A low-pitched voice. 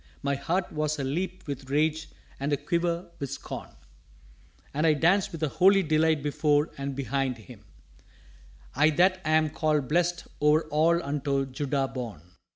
No: medium, 150 Hz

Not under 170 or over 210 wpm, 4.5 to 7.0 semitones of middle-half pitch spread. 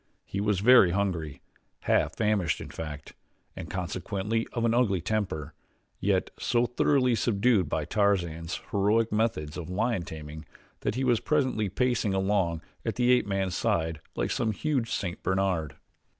No: average, 150 wpm; average, 5.2 semitones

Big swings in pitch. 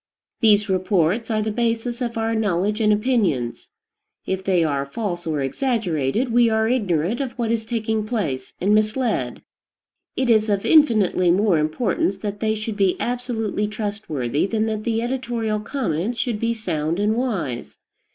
No: average, 3.9 semitones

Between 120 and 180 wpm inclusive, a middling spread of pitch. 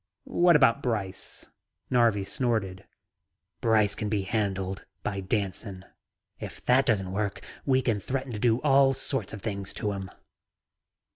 Yes: average, 140 wpm; average, 4.2 semitones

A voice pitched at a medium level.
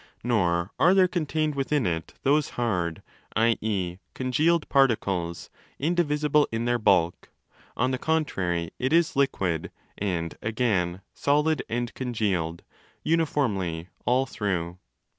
No: low, 115 Hz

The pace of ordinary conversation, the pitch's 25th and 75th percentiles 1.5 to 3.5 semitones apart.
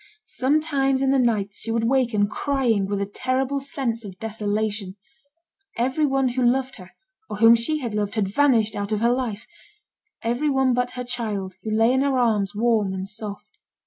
No: average, 185 wpm; average, 4.0 semitones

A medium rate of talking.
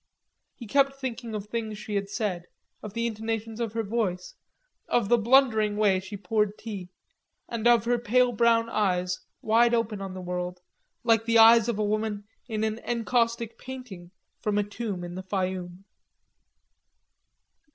Yes: average, 160 wpm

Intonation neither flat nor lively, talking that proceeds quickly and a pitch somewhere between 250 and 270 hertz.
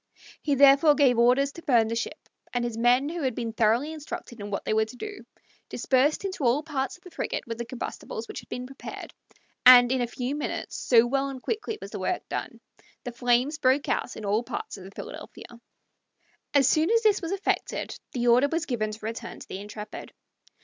Yes: average, 4.0 semitones; fast, 215 wpm; very high, 255 Hz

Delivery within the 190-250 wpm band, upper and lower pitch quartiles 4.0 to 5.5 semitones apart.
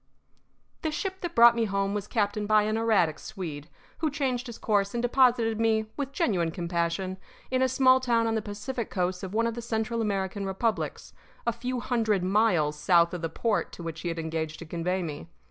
Yes: fast, 205 wpm; average, 4.8 semitones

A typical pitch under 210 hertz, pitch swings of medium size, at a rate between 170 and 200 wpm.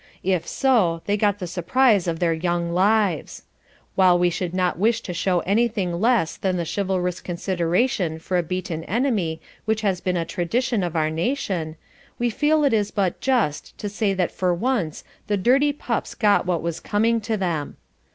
Yes: medium, 185 Hz; average, 4.4 semitones; average, 180 wpm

